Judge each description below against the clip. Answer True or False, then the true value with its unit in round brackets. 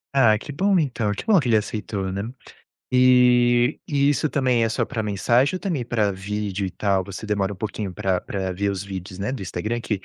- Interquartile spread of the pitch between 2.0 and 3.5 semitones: False (4.2 semitones)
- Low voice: True (110 Hz)